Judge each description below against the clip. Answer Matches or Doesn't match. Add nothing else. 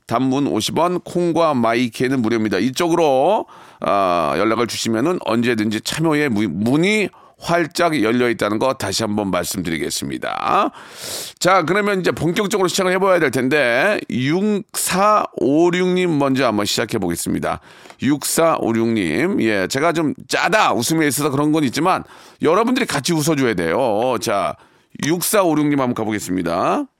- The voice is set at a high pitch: Doesn't match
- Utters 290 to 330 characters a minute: Matches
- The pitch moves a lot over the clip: Matches